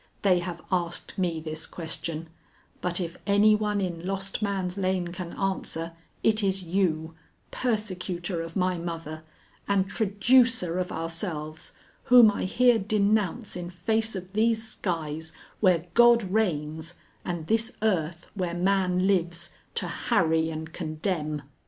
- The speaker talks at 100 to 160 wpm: Yes, slow, 135 wpm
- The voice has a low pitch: No, medium, 180 Hz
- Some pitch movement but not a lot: Yes, average, 3.4 semitones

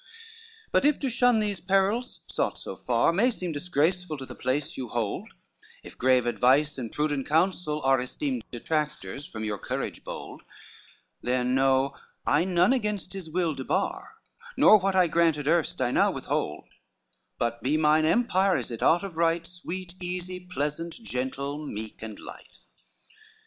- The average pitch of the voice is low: No, medium, 160 Hz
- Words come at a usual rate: Yes, average, 160 wpm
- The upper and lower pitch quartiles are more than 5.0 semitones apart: Yes, wide, 5.6 semitones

